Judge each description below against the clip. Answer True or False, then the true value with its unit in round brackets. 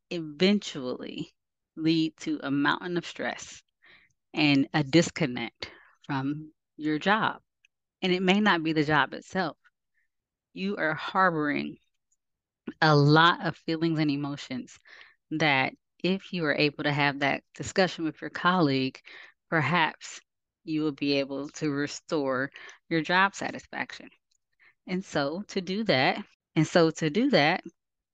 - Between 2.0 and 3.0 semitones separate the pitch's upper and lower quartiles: False (3.8 semitones)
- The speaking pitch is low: False (160 Hz)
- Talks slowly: True (130 wpm)